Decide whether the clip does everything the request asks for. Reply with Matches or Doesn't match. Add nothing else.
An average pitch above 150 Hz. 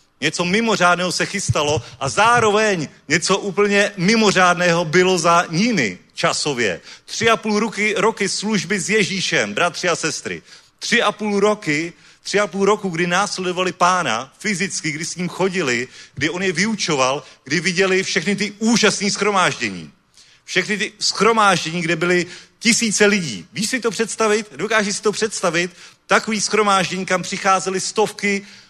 Matches